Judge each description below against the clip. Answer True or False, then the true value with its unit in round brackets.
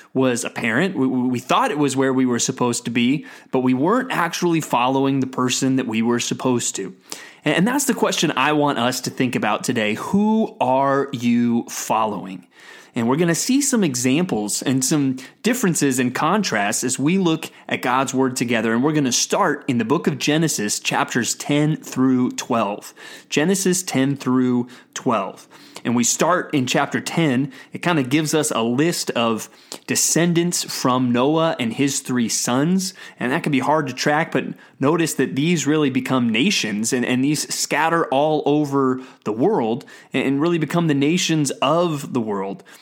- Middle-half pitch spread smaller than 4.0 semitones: False (4.3 semitones)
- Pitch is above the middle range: False (135 Hz)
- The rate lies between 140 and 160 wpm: False (180 wpm)